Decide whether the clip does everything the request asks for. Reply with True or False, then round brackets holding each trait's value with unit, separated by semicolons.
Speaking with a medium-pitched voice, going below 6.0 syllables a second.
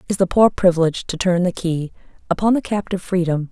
False (180 Hz; 6.4 syllables/s)